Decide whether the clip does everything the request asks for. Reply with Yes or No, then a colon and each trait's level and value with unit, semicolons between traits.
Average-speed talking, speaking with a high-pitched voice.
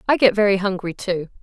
No: fast, 210 wpm; high, 195 Hz